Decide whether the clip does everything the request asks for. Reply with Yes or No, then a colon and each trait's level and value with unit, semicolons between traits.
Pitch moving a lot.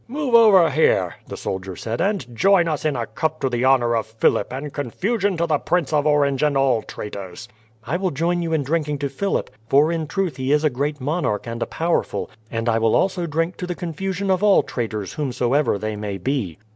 Yes: wide, 6.3 semitones